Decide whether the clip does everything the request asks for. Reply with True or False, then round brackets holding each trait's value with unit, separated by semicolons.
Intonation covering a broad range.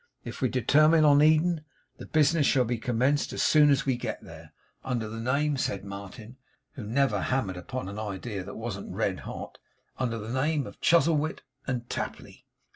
False (4.8 semitones)